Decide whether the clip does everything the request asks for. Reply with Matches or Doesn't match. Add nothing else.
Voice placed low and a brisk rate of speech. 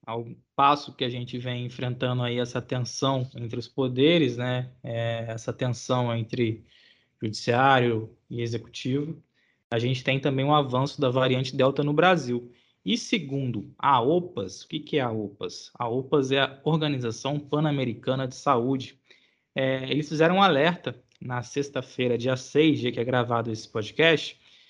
Doesn't match